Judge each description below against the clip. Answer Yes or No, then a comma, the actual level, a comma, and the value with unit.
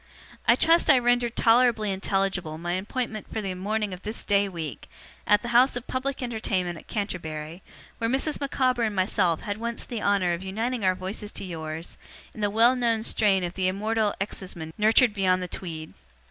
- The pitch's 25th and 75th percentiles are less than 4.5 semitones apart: Yes, average, 4.1 semitones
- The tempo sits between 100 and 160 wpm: No, average, 190 wpm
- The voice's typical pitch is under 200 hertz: No, high, 205 Hz